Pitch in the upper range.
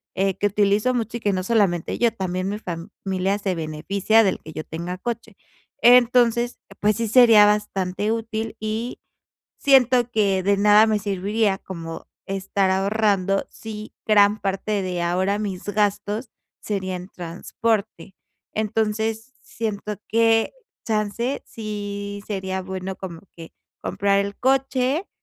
Yes: high, 205 Hz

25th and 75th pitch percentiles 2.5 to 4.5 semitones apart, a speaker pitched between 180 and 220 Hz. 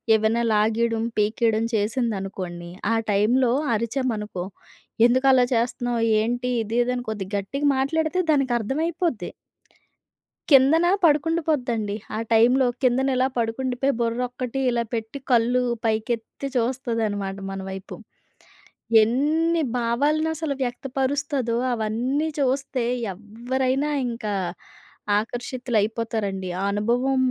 No: average, 3.4 semitones; high, 240 Hz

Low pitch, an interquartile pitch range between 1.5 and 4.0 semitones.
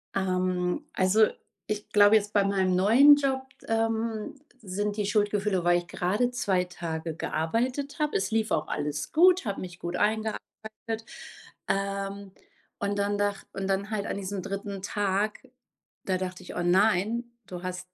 No: high, 200 Hz; average, 2.9 semitones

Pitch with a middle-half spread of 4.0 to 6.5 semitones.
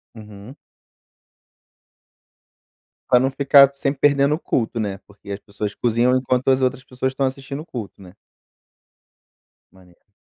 Yes: average, 4.5 semitones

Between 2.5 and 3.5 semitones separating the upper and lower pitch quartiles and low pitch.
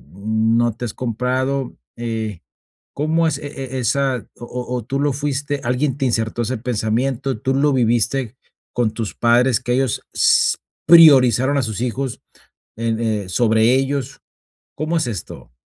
Yes: average, 3.2 semitones; low, 125 Hz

